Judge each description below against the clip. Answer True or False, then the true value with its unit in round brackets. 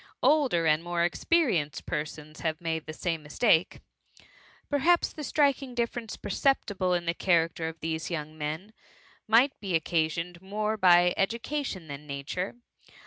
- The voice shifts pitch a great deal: True (5.8 semitones)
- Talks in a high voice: False (175 Hz)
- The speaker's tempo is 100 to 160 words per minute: True (140 wpm)